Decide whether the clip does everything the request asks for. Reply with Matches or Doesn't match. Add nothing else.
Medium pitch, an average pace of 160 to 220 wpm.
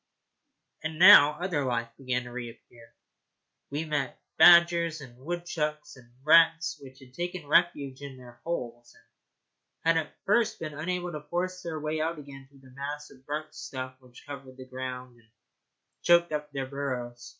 Matches